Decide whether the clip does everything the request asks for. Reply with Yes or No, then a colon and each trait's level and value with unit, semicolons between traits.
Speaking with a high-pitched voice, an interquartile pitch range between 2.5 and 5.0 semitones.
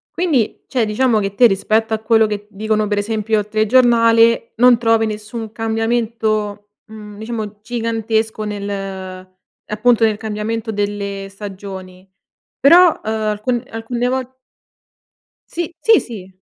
No: high, 220 Hz; narrow, 1.9 semitones